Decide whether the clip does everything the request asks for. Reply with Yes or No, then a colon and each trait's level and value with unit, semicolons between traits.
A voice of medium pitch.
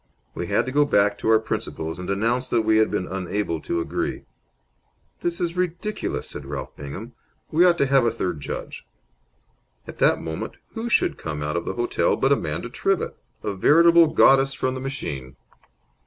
No: low, 110 Hz